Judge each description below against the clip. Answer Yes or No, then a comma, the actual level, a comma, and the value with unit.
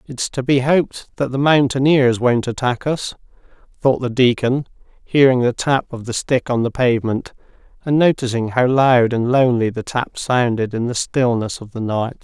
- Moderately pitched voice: No, low, 125 Hz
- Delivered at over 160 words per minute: Yes, average, 180 wpm